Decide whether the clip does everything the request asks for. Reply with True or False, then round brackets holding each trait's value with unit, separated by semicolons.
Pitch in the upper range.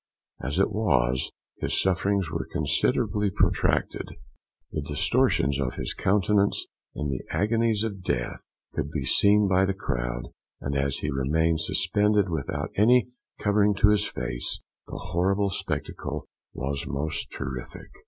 False (90 Hz)